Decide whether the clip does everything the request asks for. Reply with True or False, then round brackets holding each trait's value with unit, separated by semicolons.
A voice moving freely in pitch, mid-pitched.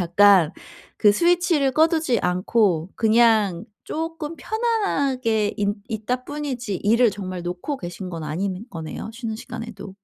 False (6.9 semitones; 220 Hz)